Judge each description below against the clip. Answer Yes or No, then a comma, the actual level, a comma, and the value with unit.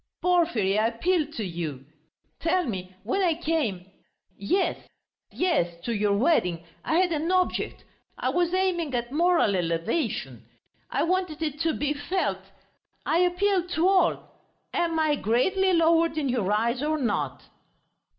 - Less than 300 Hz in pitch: No, very high, 310 Hz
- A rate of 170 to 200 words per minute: No, average, 145 wpm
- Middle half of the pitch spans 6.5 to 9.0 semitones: Yes, wide, 8.6 semitones